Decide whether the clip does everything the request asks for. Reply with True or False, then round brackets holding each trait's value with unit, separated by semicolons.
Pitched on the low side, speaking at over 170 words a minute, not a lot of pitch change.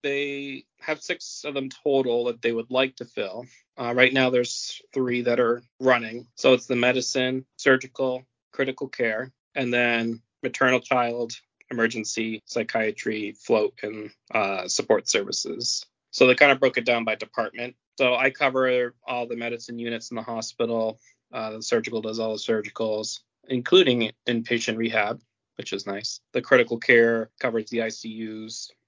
False (120 Hz; 160 wpm; 2.1 semitones)